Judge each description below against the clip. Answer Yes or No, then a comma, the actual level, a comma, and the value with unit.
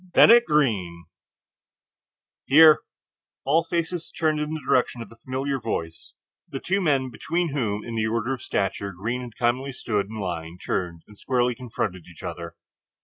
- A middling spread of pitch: No, wide, 6.5 semitones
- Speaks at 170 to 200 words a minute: No, average, 160 wpm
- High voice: No, low, 120 Hz